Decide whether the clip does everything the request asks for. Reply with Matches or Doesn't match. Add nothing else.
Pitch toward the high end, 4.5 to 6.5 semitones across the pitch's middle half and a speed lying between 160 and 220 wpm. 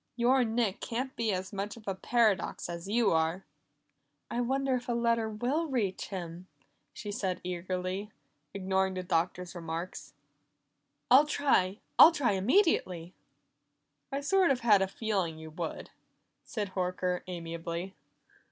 Doesn't match